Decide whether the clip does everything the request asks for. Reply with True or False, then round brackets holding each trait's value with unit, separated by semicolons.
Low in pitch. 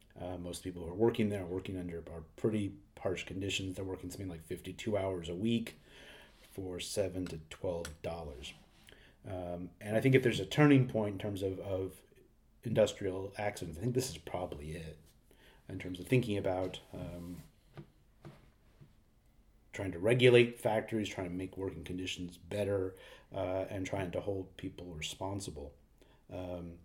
True (95 Hz)